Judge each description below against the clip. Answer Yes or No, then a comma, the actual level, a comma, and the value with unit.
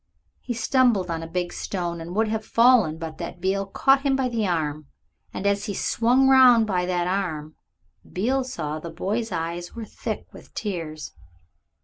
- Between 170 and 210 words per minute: Yes, average, 185 wpm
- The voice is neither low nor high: No, high, 195 Hz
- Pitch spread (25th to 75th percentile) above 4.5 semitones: Yes, wide, 5.6 semitones